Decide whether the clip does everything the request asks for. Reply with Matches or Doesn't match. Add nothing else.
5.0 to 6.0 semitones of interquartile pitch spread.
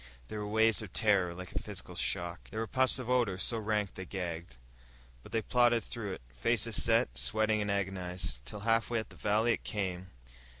Doesn't match